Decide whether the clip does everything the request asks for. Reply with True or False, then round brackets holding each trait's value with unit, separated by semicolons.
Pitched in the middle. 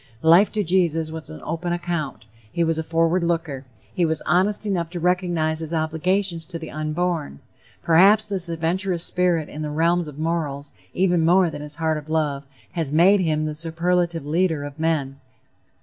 True (165 Hz)